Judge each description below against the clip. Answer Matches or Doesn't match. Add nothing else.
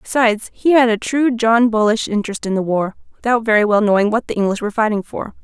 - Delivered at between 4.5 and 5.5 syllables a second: Doesn't match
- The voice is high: Matches